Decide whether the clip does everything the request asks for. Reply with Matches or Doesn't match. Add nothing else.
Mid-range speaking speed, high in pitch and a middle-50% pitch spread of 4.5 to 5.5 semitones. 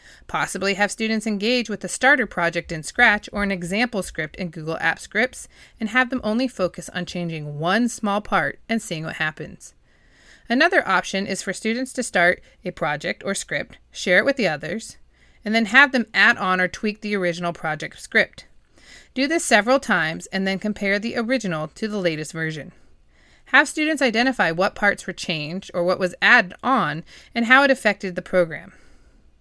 Matches